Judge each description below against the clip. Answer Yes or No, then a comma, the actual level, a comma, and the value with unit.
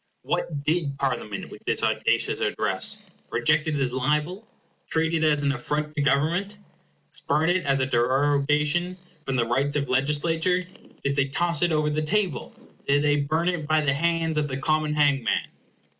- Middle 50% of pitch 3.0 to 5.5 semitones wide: No, narrow, 2.6 semitones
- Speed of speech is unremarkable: Yes, average, 175 wpm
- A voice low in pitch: No, medium, 150 Hz